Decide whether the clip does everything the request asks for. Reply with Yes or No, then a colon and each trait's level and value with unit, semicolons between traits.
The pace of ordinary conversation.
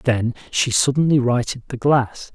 Yes: average, 155 wpm